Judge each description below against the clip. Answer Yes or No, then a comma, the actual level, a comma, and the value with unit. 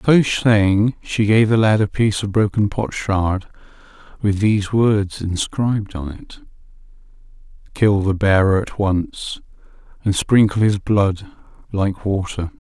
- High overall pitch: No, low, 100 Hz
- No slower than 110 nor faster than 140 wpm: Yes, slow, 135 wpm